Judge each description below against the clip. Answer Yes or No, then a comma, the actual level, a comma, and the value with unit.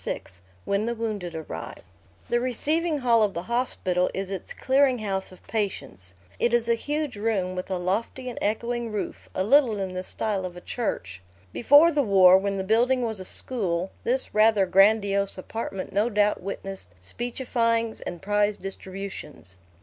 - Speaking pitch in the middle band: No, high, 210 Hz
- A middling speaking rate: Yes, average, 170 wpm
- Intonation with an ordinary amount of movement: Yes, average, 4.0 semitones